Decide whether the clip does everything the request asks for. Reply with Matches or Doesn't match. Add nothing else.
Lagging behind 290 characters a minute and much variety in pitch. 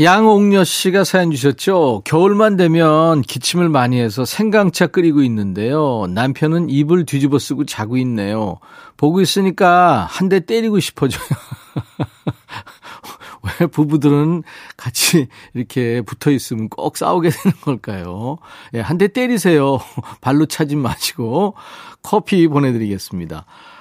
Matches